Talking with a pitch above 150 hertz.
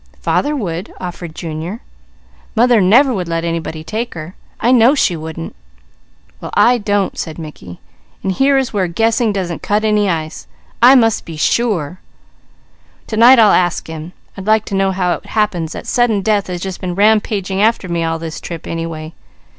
Yes: high, 190 Hz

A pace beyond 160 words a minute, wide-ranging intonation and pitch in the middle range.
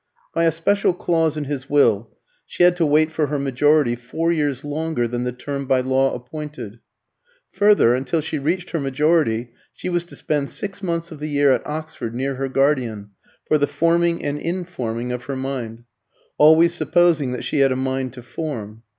No: average, 190 wpm; average, 4.2 semitones; medium, 145 Hz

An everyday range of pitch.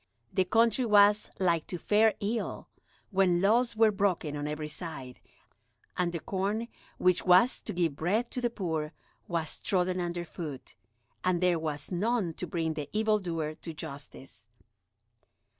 Yes: average, 4.5 semitones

